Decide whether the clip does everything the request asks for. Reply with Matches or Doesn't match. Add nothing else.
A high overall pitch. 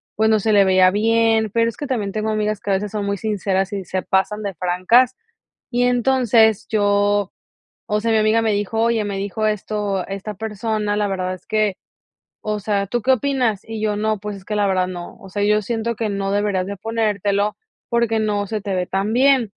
Matches